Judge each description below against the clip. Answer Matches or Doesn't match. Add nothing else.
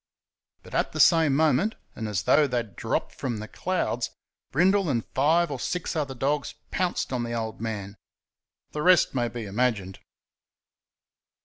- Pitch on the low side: Matches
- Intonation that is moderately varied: Doesn't match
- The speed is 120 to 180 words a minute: Matches